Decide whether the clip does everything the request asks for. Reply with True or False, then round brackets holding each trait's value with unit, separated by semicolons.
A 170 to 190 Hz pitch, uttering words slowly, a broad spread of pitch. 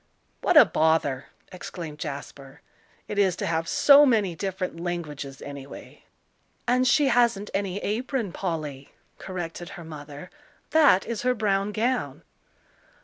True (185 Hz; 130 wpm; 5.9 semitones)